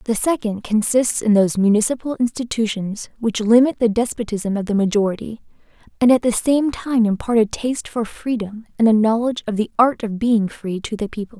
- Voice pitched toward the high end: Yes, high, 225 Hz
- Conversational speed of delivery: Yes, average, 190 wpm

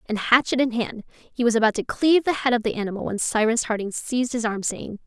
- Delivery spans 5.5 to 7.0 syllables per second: Yes, 6.0 syllables/s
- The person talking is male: No, female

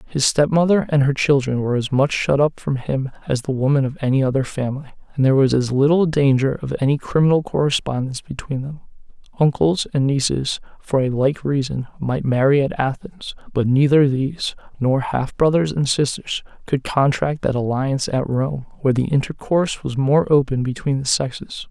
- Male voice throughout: Yes, male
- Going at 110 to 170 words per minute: No, average, 180 wpm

